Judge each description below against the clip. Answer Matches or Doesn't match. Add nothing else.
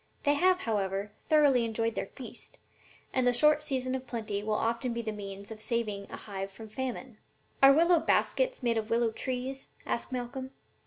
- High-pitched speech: Matches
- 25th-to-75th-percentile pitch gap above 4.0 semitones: Doesn't match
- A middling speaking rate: Matches